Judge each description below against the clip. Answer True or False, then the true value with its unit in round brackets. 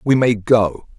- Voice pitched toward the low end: True (110 Hz)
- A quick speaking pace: False (185 wpm)